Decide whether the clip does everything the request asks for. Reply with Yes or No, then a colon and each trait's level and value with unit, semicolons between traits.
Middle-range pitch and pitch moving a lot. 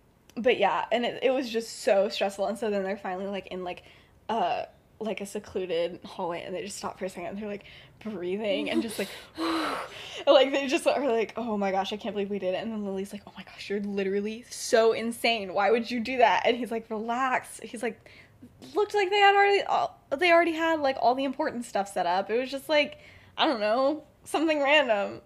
No: high, 225 Hz; wide, 6.0 semitones